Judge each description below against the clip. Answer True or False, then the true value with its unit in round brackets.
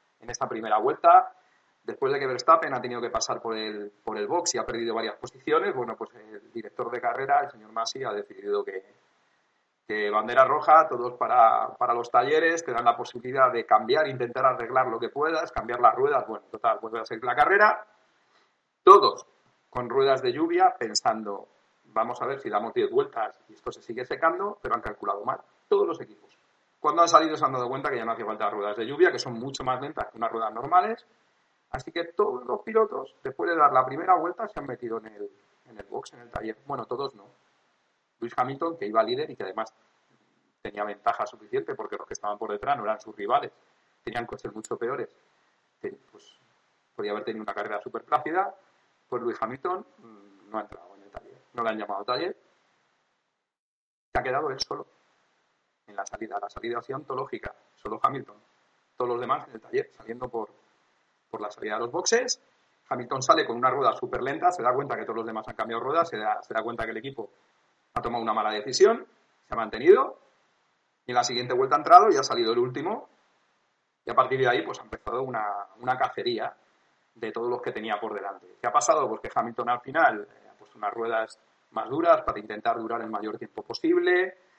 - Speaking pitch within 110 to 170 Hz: False (185 Hz)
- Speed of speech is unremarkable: False (215 wpm)